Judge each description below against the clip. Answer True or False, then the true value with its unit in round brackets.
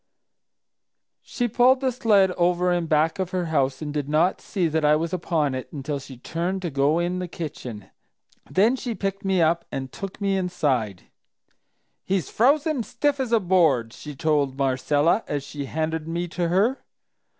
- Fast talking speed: False (180 wpm)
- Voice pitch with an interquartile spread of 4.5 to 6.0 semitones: True (4.8 semitones)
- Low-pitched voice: False (170 Hz)